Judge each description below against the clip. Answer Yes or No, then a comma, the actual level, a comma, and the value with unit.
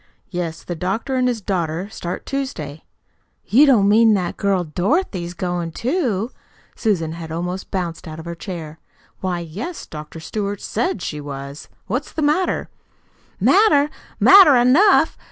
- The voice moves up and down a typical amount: No, wide, 7.0 semitones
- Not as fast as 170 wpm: Yes, average, 145 wpm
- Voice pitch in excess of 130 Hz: Yes, high, 190 Hz